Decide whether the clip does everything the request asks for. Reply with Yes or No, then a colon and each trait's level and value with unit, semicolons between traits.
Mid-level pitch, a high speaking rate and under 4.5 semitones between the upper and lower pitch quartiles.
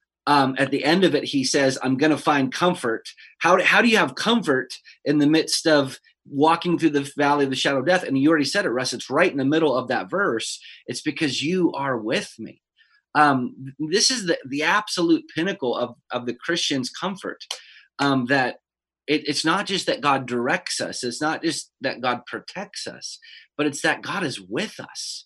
Yes: medium, 150 Hz; fast, 210 wpm; average, 3.6 semitones